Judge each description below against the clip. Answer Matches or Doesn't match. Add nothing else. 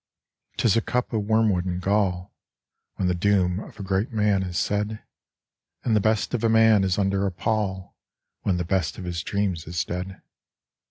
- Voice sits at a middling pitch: Doesn't match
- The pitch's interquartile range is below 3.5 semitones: Matches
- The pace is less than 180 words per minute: Doesn't match